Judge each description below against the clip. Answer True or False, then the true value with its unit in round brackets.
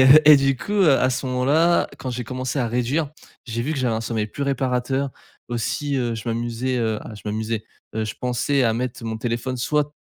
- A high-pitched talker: False (125 Hz)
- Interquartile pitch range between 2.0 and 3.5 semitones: True (3.0 semitones)